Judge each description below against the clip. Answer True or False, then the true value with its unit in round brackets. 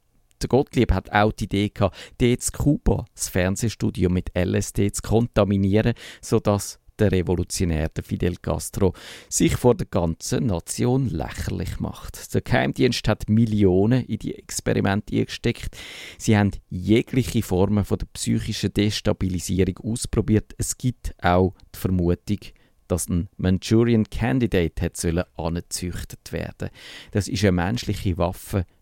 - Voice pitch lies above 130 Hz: False (100 Hz)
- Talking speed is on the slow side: True (120 wpm)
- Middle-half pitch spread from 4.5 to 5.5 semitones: False (3.9 semitones)